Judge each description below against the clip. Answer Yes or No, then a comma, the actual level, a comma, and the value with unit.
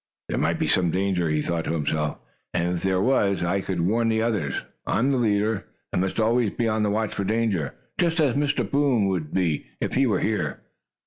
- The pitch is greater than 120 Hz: No, low, 100 Hz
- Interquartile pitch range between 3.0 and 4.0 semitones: No, average, 4.7 semitones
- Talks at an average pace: No, fast, 220 wpm